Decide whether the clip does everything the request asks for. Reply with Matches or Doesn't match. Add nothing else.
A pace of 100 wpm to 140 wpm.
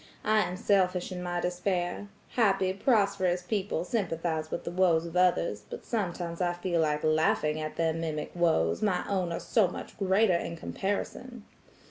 Doesn't match